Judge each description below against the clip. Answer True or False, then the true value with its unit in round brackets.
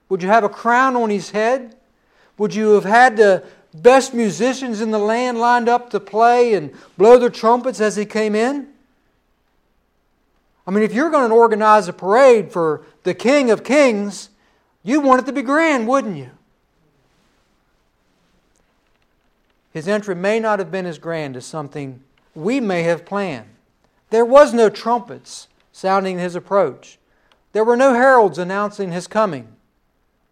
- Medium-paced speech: True (160 wpm)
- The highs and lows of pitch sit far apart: False (4.5 semitones)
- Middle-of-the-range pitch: False (215 Hz)